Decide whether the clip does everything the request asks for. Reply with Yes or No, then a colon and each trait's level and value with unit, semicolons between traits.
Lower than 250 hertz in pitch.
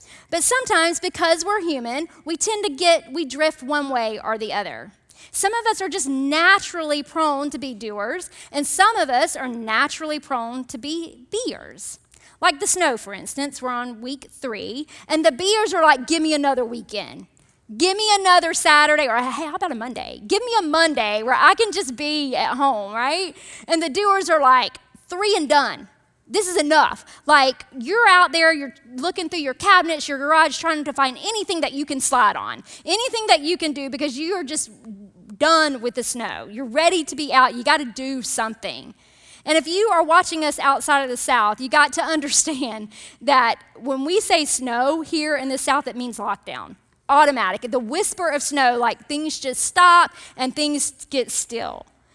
No: very high, 295 Hz